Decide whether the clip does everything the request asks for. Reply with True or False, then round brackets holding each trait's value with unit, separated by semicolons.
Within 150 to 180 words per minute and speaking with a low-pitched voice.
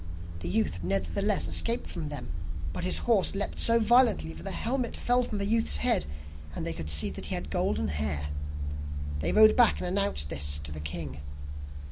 False (190 wpm; 90 Hz)